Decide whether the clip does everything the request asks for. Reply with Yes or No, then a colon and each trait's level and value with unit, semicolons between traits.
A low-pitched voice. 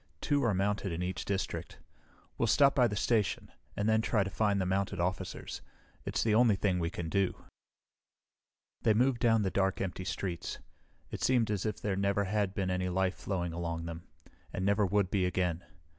Yes: low, 100 Hz